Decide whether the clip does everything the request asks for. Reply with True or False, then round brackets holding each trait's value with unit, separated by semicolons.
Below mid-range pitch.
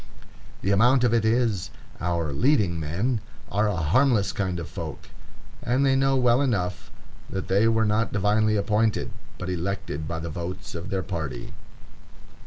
True (100 Hz)